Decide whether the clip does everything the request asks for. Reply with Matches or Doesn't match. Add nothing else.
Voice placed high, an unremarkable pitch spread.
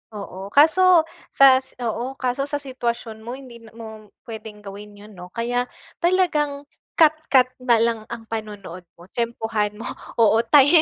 Matches